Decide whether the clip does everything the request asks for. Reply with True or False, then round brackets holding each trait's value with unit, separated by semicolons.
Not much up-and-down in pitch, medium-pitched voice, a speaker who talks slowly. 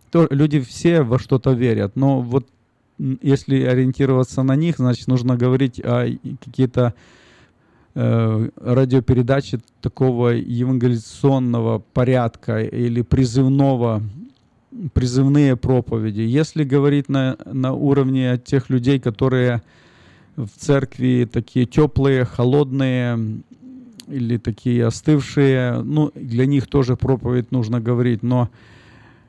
False (2.1 semitones; 130 Hz; 100 wpm)